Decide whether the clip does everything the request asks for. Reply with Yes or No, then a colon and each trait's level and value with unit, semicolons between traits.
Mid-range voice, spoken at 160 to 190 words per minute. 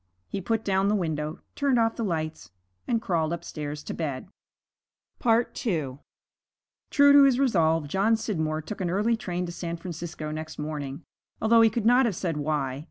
Yes: medium, 175 Hz; average, 170 wpm